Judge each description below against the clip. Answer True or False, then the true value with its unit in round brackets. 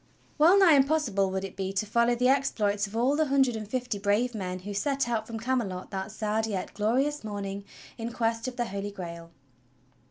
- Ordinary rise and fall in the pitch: True (4.0 semitones)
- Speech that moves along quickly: True (215 wpm)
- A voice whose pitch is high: True (220 Hz)